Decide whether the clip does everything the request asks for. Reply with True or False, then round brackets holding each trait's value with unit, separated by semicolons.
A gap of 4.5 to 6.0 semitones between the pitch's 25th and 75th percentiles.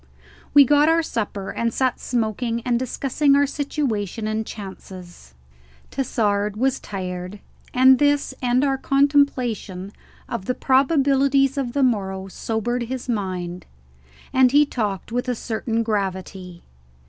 True (5.0 semitones)